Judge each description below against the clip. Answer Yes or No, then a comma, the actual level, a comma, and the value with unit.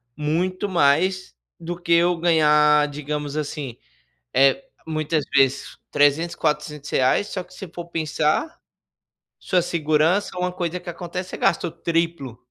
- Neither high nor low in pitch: Yes, medium, 160 Hz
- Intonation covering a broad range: No, average, 2.7 semitones